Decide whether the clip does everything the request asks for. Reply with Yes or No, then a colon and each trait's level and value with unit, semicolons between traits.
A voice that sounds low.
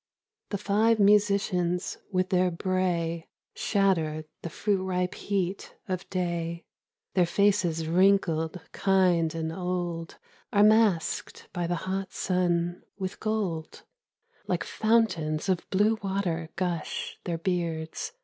No: medium, 180 Hz